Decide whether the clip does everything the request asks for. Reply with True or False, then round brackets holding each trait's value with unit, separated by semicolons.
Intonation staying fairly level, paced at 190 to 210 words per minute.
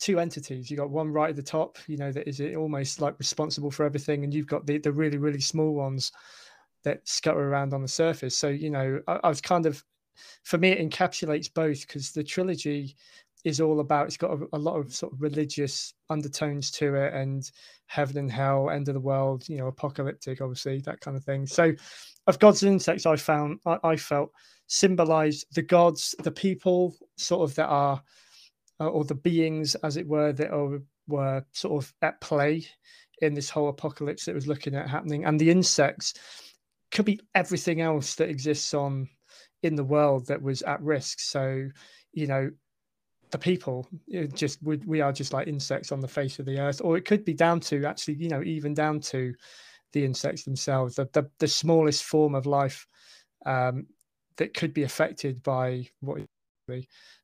True (2.2 semitones; 200 wpm)